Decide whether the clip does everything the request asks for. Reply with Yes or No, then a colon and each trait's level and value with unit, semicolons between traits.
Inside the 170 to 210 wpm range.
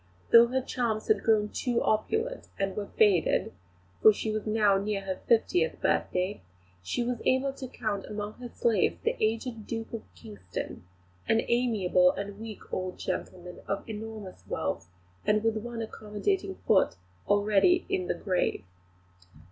No: average, 150 wpm